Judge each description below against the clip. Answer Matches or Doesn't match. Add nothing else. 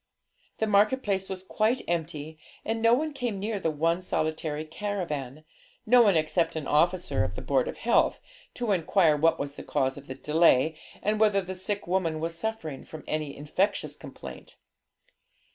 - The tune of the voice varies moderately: Matches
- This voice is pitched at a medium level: Matches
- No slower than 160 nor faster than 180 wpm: Matches